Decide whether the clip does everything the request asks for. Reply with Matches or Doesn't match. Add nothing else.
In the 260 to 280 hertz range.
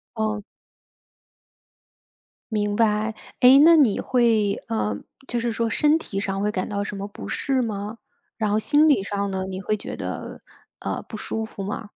Doesn't match